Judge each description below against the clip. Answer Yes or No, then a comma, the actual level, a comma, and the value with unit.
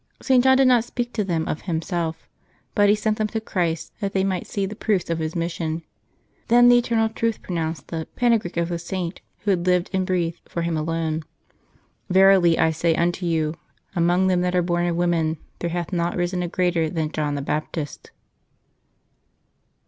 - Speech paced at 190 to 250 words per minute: Yes, average, 195 wpm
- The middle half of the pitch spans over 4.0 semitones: No, average, 3.0 semitones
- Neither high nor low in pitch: Yes, medium, 175 Hz